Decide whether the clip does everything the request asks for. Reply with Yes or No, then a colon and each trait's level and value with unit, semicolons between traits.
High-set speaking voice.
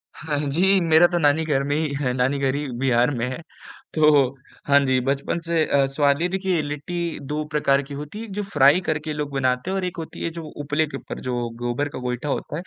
No: medium, 145 Hz